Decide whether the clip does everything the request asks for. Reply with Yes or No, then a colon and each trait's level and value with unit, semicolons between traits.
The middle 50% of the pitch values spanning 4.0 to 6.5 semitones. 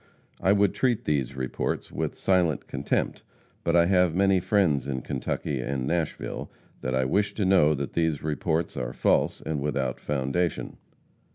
Yes: average, 5.2 semitones